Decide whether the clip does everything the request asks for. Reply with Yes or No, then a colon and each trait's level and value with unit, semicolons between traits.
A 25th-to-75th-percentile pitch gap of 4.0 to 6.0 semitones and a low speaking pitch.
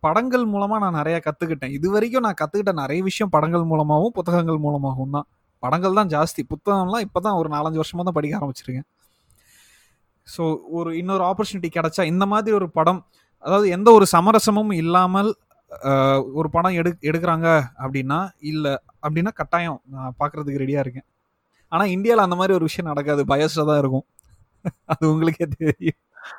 No: average, 4.3 semitones; medium, 165 Hz